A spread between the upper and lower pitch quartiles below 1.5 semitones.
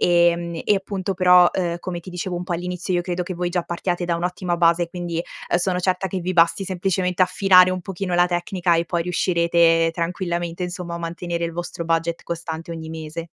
Yes: narrow, 1.1 semitones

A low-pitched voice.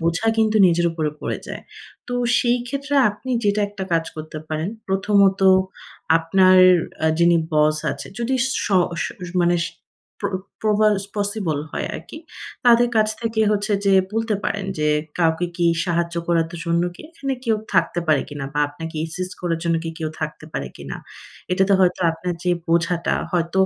No: medium, 180 Hz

